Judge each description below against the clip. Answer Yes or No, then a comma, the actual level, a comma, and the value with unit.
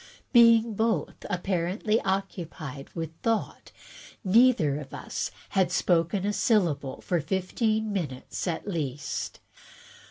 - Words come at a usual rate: No, slow, 105 wpm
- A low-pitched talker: No, medium, 185 Hz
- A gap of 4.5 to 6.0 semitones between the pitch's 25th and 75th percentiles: Yes, average, 5.0 semitones